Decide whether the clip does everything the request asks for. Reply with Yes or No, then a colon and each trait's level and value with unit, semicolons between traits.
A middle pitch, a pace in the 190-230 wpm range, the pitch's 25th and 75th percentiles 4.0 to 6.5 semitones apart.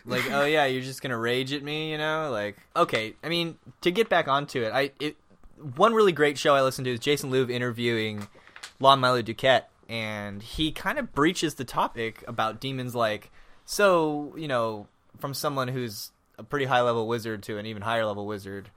No: low, 130 Hz; fast, 205 wpm; average, 4.9 semitones